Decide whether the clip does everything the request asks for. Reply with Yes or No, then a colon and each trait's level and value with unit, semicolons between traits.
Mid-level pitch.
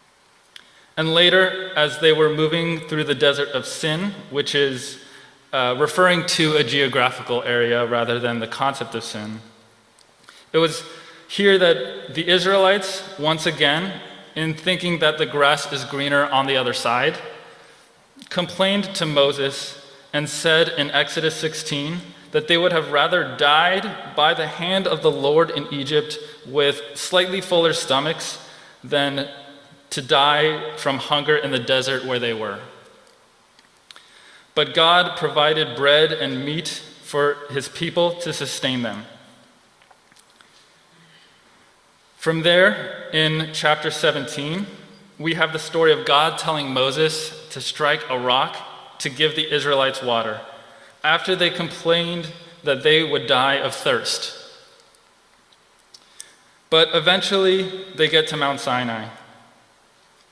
Yes: medium, 155 Hz